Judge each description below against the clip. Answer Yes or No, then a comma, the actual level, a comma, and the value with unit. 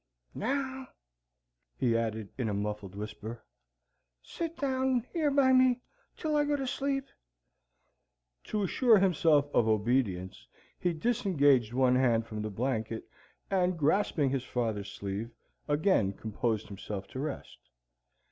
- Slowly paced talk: Yes, slow, 125 wpm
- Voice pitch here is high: No, low, 135 Hz